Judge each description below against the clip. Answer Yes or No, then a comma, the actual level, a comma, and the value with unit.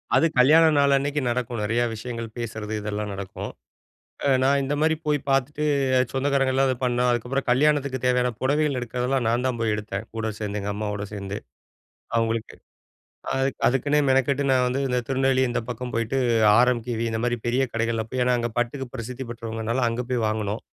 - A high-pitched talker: No, low, 125 Hz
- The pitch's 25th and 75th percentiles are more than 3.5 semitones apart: No, average, 2.9 semitones